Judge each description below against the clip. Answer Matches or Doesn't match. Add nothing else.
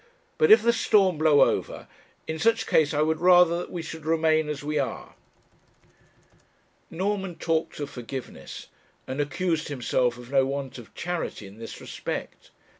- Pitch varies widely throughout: Doesn't match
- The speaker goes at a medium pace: Matches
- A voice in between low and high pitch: Matches